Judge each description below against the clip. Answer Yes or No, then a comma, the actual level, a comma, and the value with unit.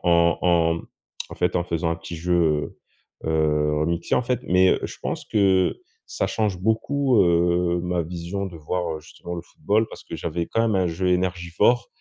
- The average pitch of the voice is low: Yes, very low, 85 Hz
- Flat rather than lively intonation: Yes, narrow, 2.0 semitones